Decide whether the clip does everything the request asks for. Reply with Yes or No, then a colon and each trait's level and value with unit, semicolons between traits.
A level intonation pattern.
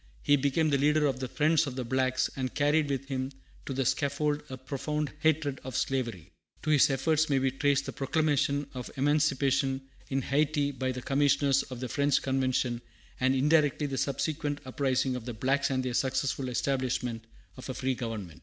Yes: narrow, 1.9 semitones